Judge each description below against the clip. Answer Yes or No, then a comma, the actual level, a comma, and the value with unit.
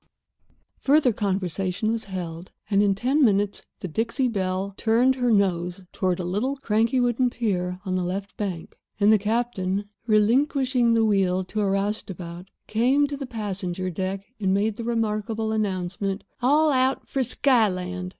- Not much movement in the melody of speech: No, average, 4.1 semitones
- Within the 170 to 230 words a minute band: No, average, 155 wpm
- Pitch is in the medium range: No, high, 205 Hz